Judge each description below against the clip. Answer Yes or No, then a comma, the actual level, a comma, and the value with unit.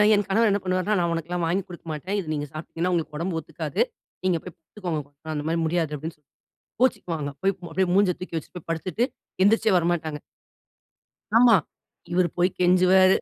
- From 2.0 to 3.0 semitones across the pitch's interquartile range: Yes, average, 2.7 semitones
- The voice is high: No, medium, 175 Hz